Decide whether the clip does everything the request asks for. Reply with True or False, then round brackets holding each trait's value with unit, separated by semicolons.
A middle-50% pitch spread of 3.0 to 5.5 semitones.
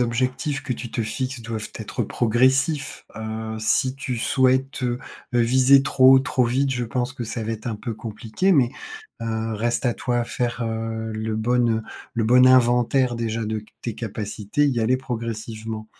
False (2.4 semitones)